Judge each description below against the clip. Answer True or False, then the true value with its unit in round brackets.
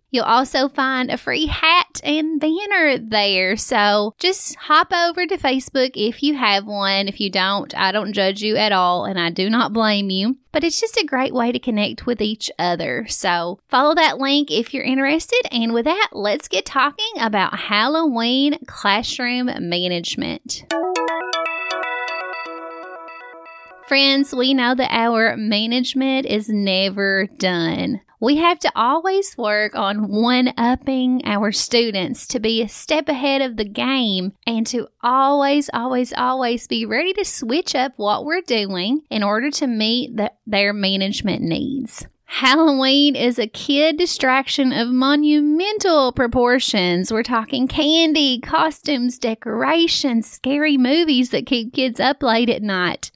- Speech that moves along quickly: False (150 wpm)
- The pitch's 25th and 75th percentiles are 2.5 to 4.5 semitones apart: False (5.3 semitones)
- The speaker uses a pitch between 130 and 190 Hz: False (245 Hz)